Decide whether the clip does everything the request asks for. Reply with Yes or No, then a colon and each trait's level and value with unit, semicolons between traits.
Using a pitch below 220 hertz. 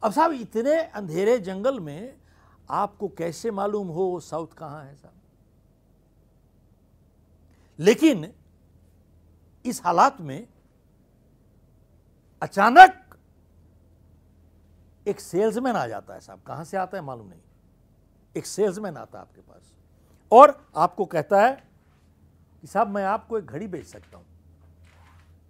Yes: low, 135 Hz